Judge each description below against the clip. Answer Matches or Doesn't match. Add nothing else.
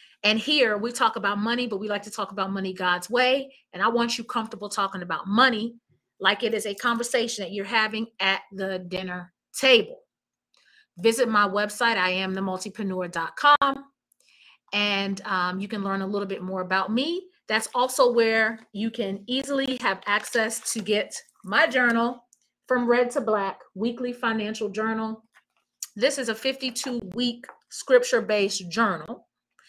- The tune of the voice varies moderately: Matches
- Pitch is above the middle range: Matches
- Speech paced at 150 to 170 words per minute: Matches